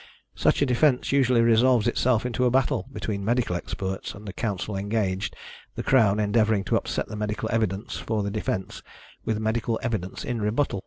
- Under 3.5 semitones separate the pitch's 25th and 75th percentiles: Yes, average, 3.0 semitones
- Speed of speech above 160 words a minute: Yes, average, 175 wpm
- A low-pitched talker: Yes, low, 110 Hz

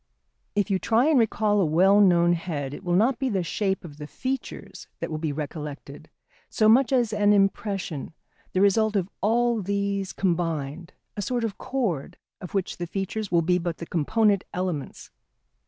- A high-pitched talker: Yes, high, 195 Hz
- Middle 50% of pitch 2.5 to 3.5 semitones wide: No, average, 4.1 semitones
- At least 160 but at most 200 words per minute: Yes, average, 185 wpm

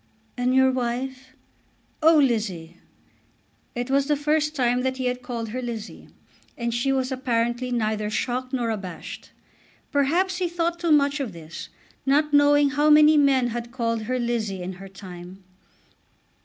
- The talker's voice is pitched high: Yes, very high, 255 Hz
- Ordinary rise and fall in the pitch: Yes, average, 3.7 semitones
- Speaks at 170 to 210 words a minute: No, average, 155 wpm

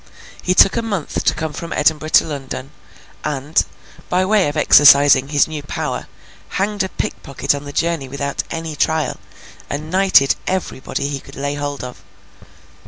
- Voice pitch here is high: No, medium, 150 Hz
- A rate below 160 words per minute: No, average, 165 wpm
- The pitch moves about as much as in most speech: Yes, average, 3.2 semitones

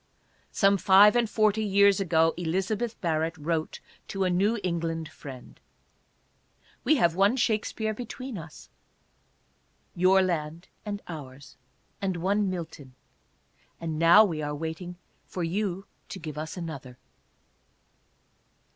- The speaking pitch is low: No, medium, 180 Hz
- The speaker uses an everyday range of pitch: Yes, average, 3.9 semitones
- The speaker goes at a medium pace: No, slow, 130 wpm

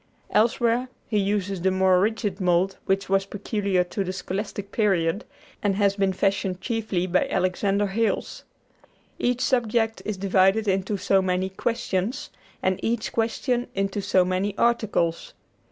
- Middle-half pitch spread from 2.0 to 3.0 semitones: Yes, average, 2.7 semitones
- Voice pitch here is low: No, high, 195 Hz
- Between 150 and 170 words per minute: No, average, 140 wpm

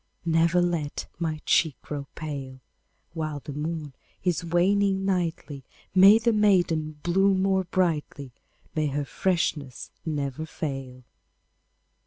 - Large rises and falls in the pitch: No, average, 4.0 semitones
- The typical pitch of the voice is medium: Yes, medium, 165 Hz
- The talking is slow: Yes, slow, 115 wpm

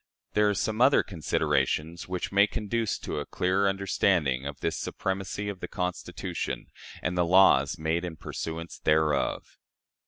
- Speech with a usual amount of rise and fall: Yes, average, 3.8 semitones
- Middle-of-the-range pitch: No, very low, 90 Hz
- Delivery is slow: No, average, 155 wpm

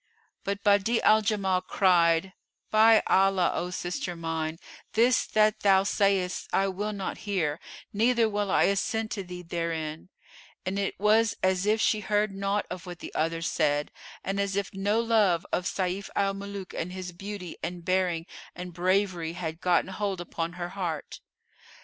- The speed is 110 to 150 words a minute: No, average, 165 wpm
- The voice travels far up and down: No, narrow, 2.5 semitones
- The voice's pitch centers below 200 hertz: Yes, high, 190 Hz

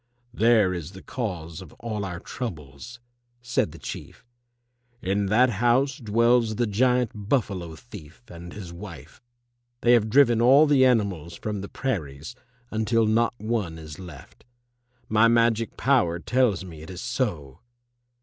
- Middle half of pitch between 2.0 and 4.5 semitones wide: No, wide, 5.4 semitones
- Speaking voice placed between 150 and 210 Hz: No, low, 110 Hz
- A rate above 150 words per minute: No, average, 145 wpm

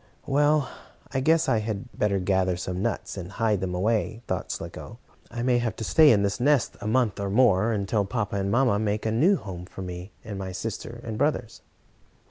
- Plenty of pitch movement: No, average, 3.7 semitones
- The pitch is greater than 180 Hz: No, low, 110 Hz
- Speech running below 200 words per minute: No, fast, 205 wpm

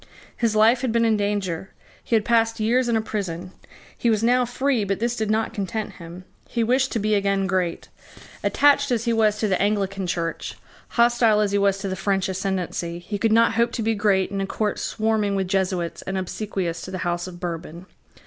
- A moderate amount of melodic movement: Yes, average, 3.1 semitones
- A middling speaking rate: No, fast, 215 wpm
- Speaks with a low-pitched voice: No, high, 205 Hz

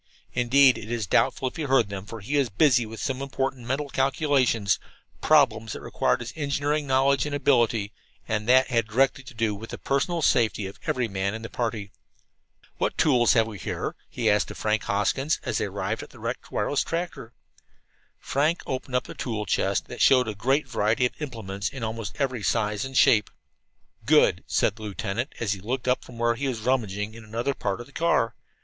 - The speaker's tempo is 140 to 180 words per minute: No, fast, 205 wpm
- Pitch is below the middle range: Yes, low, 120 Hz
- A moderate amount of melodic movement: Yes, average, 3.8 semitones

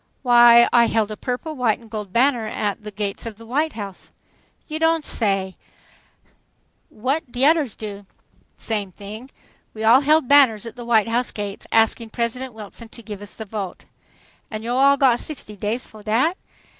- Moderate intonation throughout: Yes, average, 3.2 semitones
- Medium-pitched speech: No, high, 230 Hz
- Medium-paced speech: Yes, average, 180 wpm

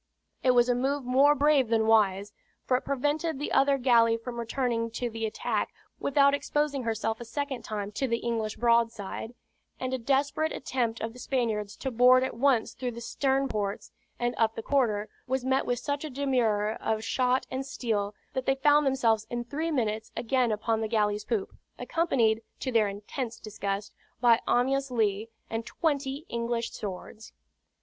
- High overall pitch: Yes, high, 240 Hz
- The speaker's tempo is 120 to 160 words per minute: No, average, 175 wpm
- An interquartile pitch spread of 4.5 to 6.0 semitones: No, average, 3.3 semitones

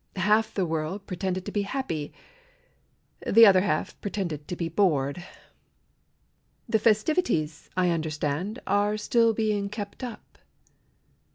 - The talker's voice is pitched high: Yes, high, 195 Hz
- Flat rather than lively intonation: No, average, 4.5 semitones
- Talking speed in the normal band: No, slow, 120 wpm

